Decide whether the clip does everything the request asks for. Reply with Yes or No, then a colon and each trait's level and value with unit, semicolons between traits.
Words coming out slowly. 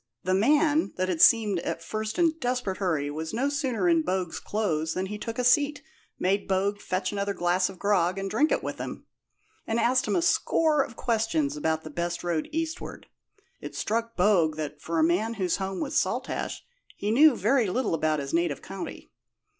No: average, 200 wpm